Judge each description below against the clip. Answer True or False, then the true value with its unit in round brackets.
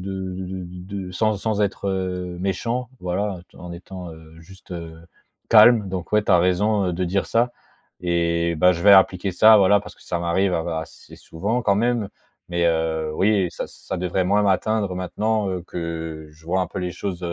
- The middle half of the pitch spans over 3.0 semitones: False (2.7 semitones)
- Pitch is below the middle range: True (95 Hz)